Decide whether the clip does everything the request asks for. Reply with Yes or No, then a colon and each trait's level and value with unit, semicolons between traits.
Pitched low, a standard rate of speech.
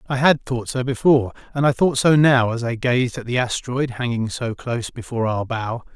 No: low, 125 Hz; fast, 220 wpm